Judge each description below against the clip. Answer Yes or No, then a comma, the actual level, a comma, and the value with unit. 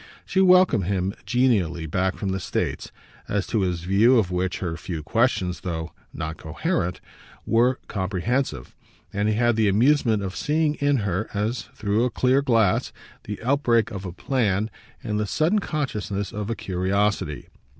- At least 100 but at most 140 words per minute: No, average, 160 wpm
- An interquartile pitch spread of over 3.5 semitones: Yes, average, 5.0 semitones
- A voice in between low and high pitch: No, low, 105 Hz